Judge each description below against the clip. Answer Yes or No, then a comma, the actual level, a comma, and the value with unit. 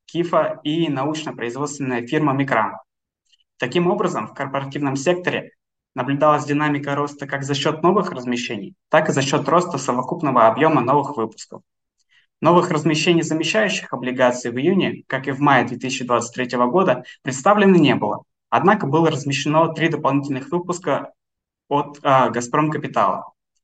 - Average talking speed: Yes, average, 130 wpm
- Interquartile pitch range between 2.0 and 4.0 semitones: Yes, average, 3.4 semitones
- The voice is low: No, medium, 145 Hz